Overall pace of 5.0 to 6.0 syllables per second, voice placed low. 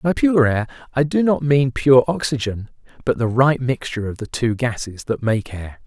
No: 4.8 syllables/s; low, 125 Hz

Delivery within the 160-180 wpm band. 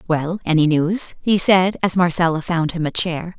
Yes: average, 175 wpm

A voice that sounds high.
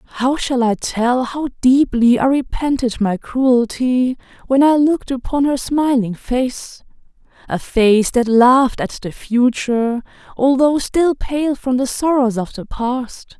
Yes: very high, 255 Hz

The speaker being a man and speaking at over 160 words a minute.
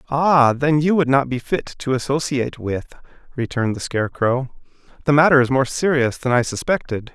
Yes: male; average, 175 wpm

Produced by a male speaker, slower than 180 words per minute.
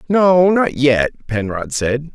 Yes: male; average, 140 wpm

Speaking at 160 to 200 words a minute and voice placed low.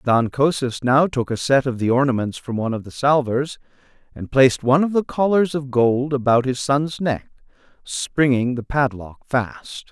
Yes: average, 180 wpm; low, 130 Hz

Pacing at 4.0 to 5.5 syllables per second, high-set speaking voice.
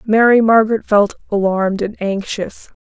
Yes: 4.8 syllables/s; high, 210 Hz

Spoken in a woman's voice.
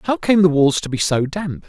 No: male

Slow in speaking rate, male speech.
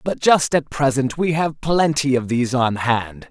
No: average, 200 wpm; male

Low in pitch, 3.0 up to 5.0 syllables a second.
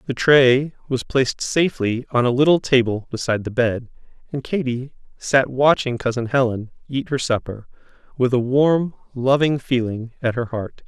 Yes: low, 130 Hz; 4.8 syllables/s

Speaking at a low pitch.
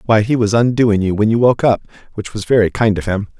Yes: low, 110 Hz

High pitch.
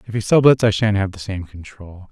No: low, 100 Hz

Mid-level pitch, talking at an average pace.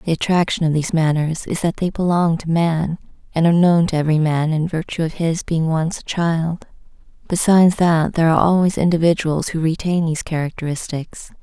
Yes: medium, 165 Hz; average, 185 wpm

